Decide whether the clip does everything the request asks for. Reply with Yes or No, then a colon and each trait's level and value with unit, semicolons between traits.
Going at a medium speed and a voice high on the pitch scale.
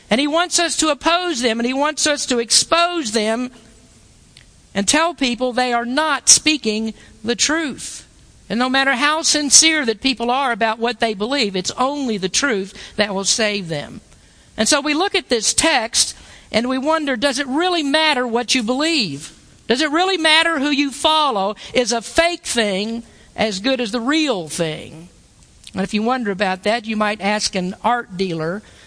Yes: average, 185 wpm; high, 245 Hz